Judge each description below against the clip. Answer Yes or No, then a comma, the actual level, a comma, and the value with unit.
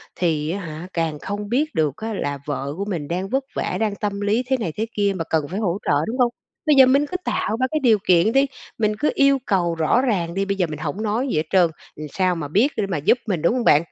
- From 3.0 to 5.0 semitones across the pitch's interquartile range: No, wide, 5.5 semitones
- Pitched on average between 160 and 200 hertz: Yes, high, 195 Hz